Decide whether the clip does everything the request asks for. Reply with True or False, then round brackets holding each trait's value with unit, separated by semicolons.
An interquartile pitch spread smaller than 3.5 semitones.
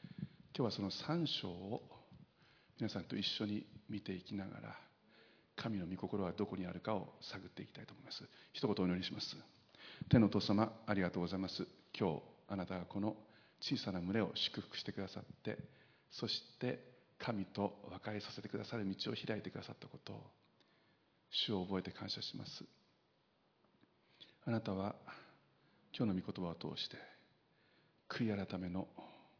True (2.5 semitones)